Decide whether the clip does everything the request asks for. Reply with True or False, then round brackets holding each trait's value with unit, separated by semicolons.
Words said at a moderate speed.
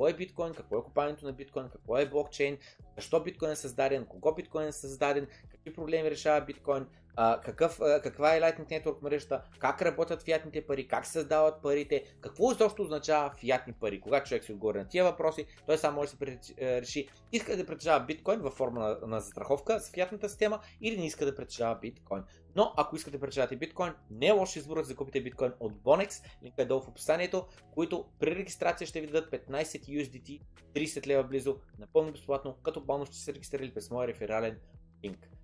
False (200 wpm)